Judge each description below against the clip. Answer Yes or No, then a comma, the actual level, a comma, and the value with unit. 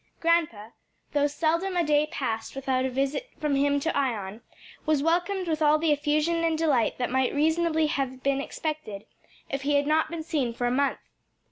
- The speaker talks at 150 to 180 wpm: No, average, 190 wpm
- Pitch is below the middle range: No, very high, 295 Hz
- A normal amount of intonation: Yes, average, 3.2 semitones